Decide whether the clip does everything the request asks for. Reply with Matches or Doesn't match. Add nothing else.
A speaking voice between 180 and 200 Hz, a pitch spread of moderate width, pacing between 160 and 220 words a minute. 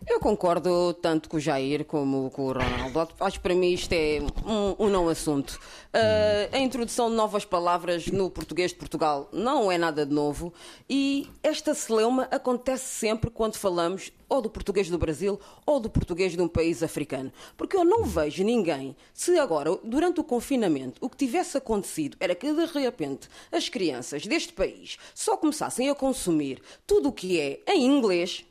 Doesn't match